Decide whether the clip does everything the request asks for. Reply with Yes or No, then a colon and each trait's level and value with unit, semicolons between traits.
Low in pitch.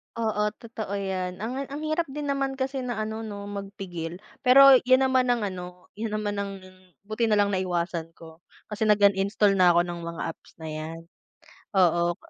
No: high, 205 Hz